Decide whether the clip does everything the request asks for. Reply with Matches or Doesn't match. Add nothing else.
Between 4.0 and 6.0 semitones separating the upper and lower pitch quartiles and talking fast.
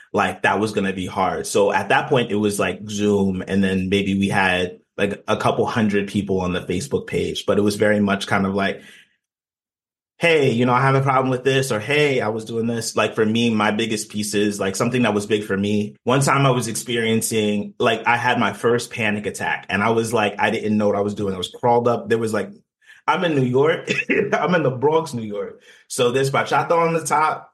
Doesn't match